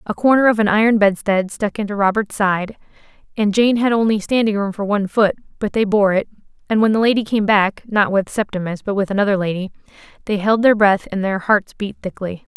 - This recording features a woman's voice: Yes, female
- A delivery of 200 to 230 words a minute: Yes, fast, 205 wpm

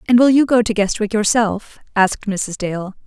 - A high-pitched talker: Yes, high, 215 Hz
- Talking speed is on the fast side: No, average, 195 wpm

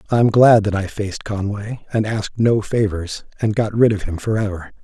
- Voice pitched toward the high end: No, low, 105 Hz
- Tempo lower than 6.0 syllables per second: Yes, 5.4 syllables/s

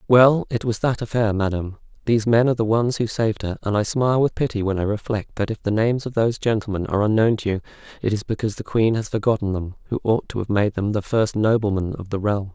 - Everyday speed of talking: No, fast, 255 wpm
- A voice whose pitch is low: Yes, low, 110 Hz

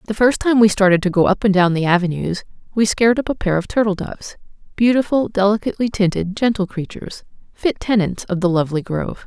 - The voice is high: Yes, high, 200 Hz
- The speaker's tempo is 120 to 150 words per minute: No, average, 200 wpm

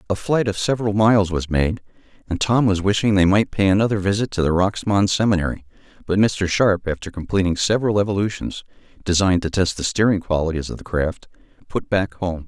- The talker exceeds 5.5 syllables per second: Yes, 5.9 syllables/s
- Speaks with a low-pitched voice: Yes, very low, 95 Hz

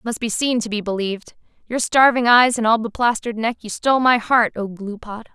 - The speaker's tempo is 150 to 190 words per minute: No, average, 200 wpm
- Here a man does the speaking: No, female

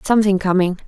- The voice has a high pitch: Yes, high, 195 Hz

